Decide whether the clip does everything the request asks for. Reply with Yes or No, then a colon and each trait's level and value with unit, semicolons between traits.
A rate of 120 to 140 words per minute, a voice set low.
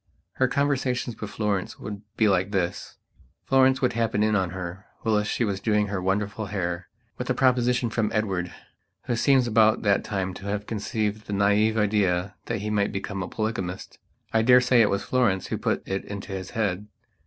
No: average, 190 wpm; low, 105 Hz